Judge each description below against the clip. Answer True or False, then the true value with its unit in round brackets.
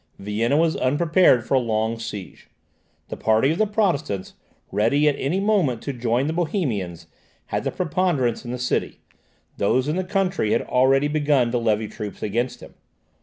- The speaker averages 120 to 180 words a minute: True (170 wpm)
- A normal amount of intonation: False (6.0 semitones)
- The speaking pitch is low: True (130 Hz)